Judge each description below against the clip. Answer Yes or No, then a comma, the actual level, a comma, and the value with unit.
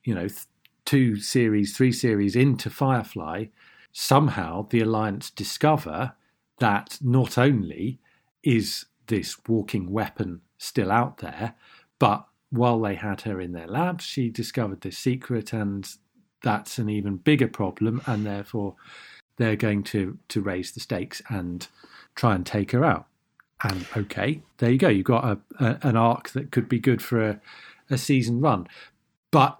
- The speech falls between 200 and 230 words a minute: No, average, 155 wpm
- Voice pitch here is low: Yes, low, 115 Hz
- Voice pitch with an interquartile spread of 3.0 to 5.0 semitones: Yes, average, 3.7 semitones